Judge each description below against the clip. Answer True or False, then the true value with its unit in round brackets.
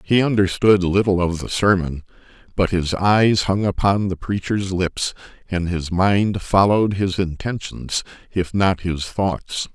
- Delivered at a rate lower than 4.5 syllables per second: True (4.0 syllables/s)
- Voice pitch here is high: False (95 Hz)